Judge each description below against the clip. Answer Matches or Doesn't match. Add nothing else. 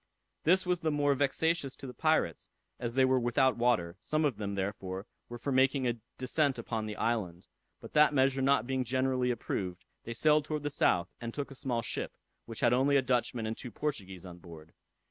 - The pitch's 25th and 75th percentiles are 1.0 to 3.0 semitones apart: Doesn't match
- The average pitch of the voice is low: Matches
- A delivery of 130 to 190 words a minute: Doesn't match